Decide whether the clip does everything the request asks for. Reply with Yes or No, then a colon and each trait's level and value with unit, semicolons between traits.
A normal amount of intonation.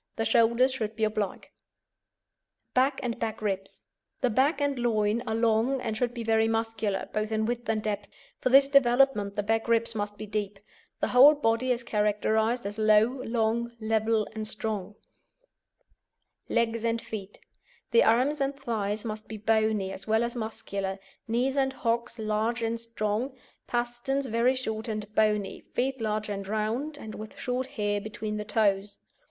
No: narrow, 2.2 semitones